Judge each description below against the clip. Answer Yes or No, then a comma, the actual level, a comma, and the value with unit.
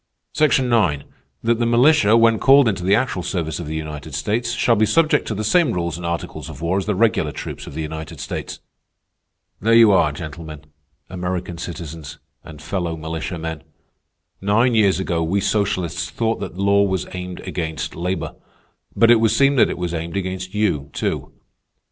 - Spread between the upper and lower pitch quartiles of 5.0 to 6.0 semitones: Yes, wide, 5.4 semitones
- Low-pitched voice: Yes, very low, 95 Hz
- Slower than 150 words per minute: No, average, 180 wpm